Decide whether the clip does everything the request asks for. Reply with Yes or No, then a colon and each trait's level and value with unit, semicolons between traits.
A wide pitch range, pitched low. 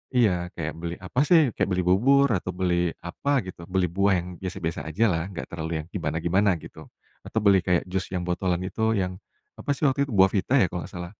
No: average, 2.7 semitones; very low, 90 Hz